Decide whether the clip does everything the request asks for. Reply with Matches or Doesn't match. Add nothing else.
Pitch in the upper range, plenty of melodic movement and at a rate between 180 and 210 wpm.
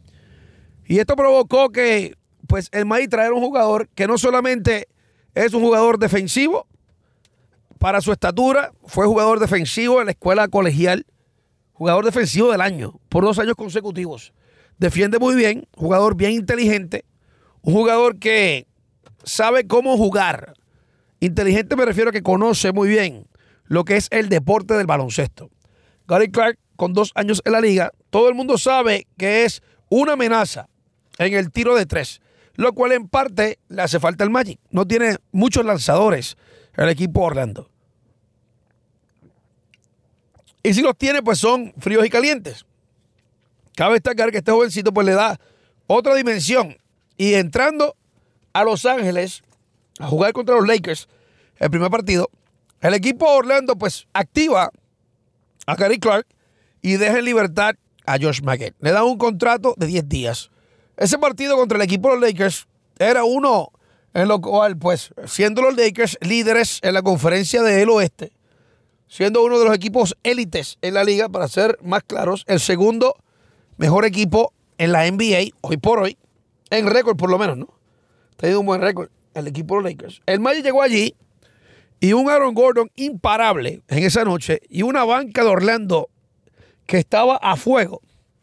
Doesn't match